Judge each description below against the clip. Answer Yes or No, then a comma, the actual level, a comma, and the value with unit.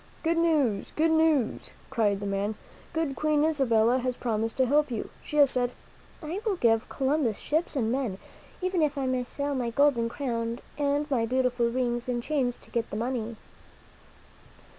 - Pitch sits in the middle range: No, very high, 255 Hz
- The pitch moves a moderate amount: Yes, average, 4.2 semitones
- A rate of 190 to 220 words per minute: No, average, 180 wpm